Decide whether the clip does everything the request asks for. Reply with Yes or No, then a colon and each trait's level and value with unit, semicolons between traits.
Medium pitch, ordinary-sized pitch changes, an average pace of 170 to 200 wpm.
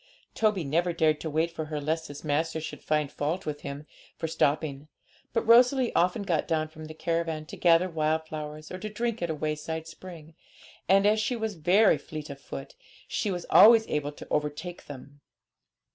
Yes: medium, 160 Hz; average, 3.2 semitones; average, 190 wpm